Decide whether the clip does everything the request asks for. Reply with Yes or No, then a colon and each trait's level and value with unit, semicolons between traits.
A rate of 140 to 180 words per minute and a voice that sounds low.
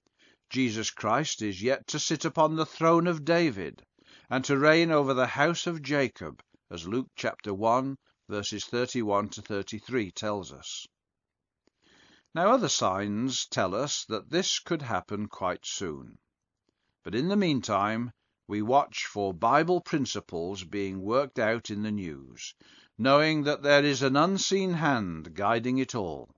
Yes: average, 150 wpm; low, 125 Hz